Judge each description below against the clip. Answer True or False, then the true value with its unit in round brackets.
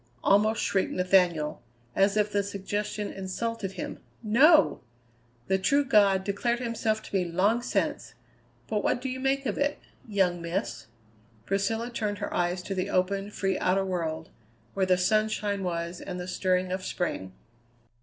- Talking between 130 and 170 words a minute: True (155 wpm)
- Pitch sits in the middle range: False (195 Hz)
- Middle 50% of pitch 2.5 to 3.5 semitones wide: True (2.9 semitones)